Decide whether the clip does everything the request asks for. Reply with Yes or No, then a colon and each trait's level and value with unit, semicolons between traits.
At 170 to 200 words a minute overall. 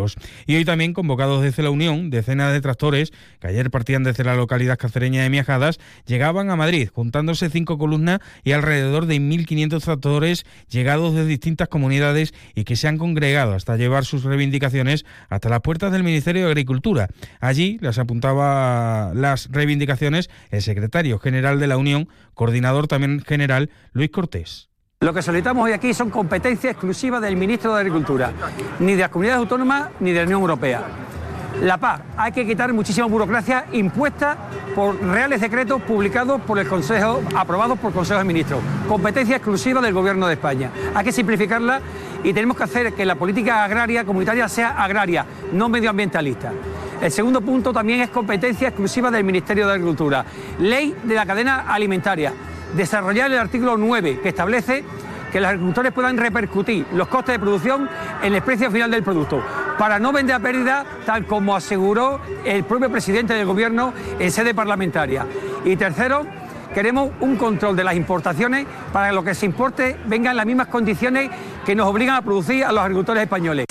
Yes: average, 175 wpm